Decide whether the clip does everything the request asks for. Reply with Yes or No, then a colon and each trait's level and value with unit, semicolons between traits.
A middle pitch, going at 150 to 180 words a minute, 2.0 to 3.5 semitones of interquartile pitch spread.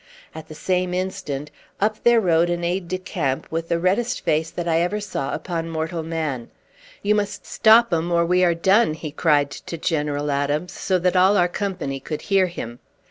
No: medium, 170 Hz; average, 195 wpm; average, 3.1 semitones